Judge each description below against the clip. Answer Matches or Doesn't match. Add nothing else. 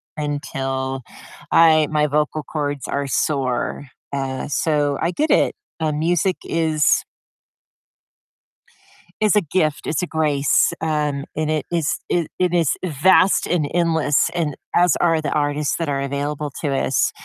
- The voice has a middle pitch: Matches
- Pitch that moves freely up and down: Doesn't match